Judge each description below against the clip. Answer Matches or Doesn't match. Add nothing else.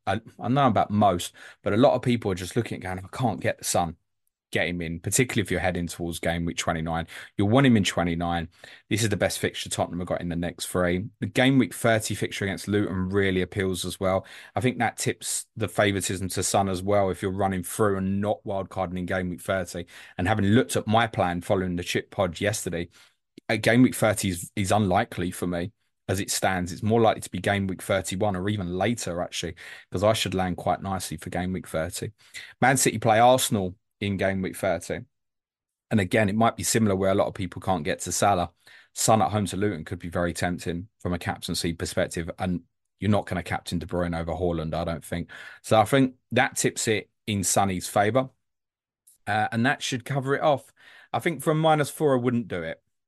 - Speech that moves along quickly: Matches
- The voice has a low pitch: Matches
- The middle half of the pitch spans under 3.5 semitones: Doesn't match